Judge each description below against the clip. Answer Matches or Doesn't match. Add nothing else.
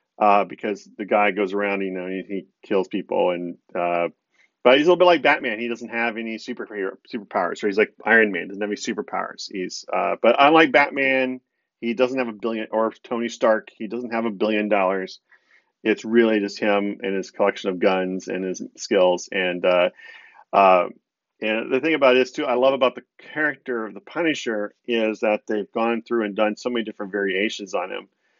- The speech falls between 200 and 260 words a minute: Matches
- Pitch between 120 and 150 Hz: Doesn't match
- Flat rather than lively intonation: Doesn't match